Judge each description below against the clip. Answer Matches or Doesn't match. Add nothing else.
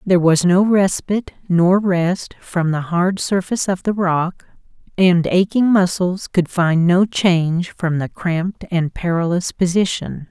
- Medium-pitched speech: Matches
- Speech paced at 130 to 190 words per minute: Matches